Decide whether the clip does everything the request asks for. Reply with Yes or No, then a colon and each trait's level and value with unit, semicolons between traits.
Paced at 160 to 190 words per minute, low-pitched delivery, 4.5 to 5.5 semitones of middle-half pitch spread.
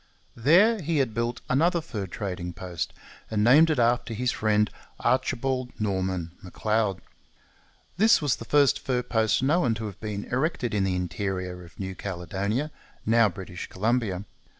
No: average, 150 wpm; low, 110 Hz; average, 5.2 semitones